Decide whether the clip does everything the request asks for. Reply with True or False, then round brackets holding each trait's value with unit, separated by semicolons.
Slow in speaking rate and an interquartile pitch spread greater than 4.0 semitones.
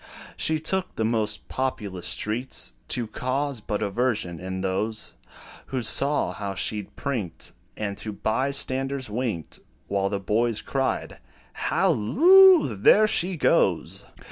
True (125 wpm; 5.1 semitones)